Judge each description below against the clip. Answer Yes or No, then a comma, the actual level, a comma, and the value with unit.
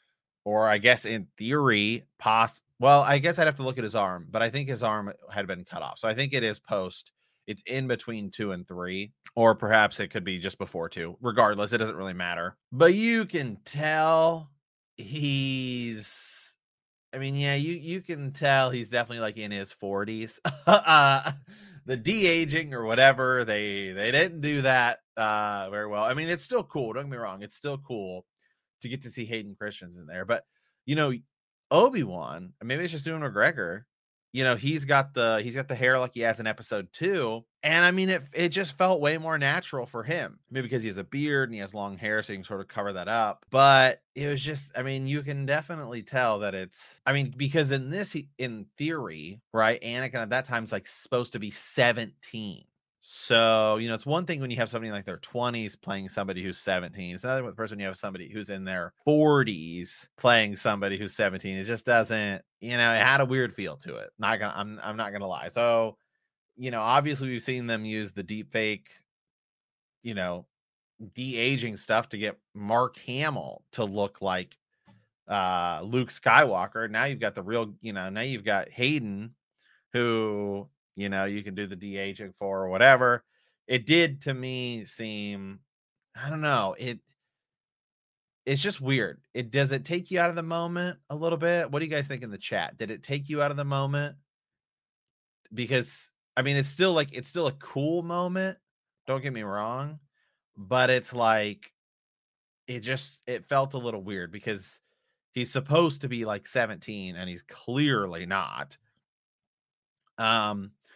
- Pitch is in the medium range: No, low, 120 Hz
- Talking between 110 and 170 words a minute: No, average, 195 wpm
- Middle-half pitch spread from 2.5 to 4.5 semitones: No, average, 5.0 semitones